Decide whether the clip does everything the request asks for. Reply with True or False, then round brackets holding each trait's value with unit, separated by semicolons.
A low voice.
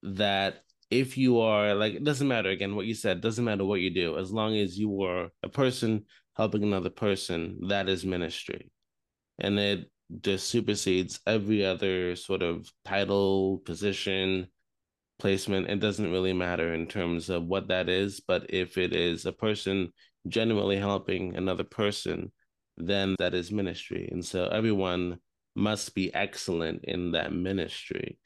True (95 Hz)